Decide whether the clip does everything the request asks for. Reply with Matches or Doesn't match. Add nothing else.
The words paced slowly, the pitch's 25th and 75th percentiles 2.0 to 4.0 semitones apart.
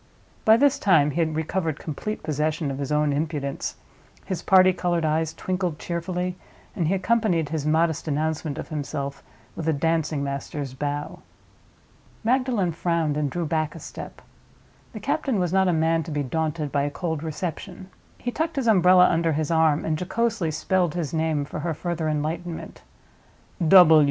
Doesn't match